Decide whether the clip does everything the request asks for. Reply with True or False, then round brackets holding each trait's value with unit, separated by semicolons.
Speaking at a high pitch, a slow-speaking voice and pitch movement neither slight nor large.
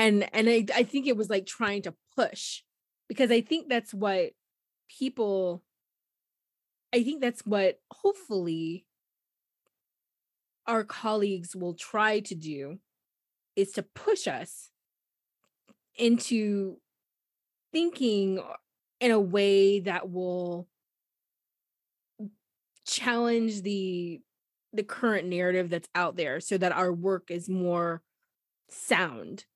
True (200 Hz; 110 wpm; 4.3 semitones)